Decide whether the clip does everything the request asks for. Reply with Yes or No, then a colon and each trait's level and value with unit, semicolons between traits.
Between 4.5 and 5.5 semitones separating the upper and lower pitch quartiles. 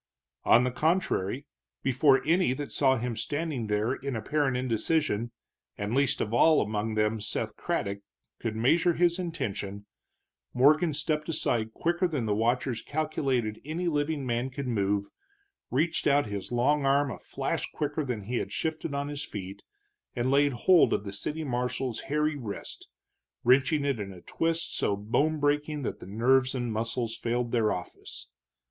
Yes: average, 5.0 semitones